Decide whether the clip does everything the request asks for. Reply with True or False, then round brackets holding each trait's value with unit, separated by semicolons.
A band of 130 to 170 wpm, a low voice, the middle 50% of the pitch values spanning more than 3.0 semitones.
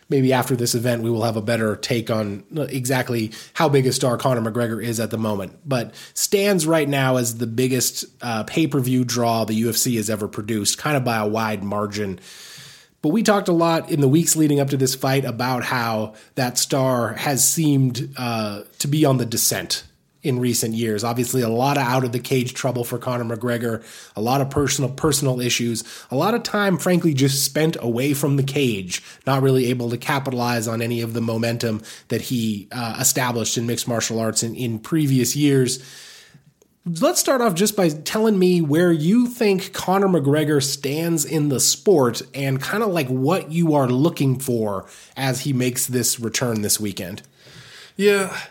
False (190 wpm; 130 Hz; 4.1 semitones)